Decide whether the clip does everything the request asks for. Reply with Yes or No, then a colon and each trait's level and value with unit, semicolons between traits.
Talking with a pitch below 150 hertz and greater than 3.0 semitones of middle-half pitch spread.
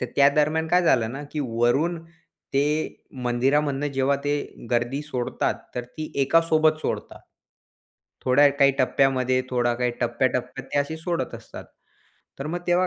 Yes: medium, 140 Hz; average, 3.6 semitones